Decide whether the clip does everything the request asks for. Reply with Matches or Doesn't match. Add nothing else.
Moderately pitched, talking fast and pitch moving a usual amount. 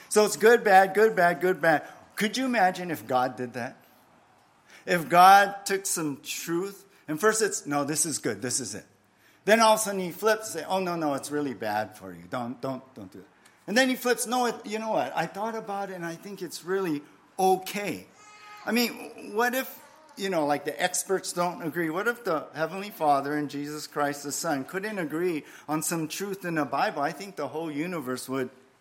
Doesn't match